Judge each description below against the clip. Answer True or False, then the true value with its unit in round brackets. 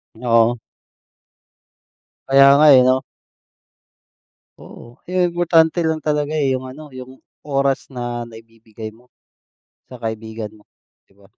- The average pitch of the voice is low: True (130 Hz)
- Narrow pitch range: False (4.5 semitones)